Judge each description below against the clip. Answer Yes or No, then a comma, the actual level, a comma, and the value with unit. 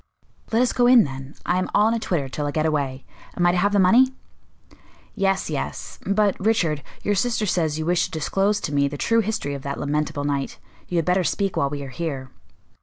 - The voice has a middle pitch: Yes, medium, 170 Hz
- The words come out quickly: Yes, fast, 230 wpm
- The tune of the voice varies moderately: No, wide, 6.0 semitones